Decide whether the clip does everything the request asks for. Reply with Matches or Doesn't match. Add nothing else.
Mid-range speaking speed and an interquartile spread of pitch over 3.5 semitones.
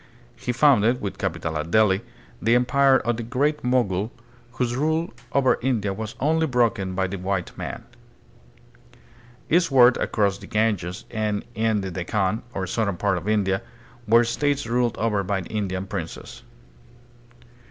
Matches